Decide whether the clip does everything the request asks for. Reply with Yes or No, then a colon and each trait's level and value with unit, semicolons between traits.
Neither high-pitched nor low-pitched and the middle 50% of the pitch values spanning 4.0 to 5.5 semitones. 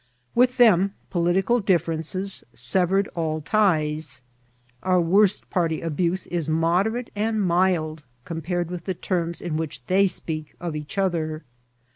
No: medium, 175 Hz; average, 3.2 semitones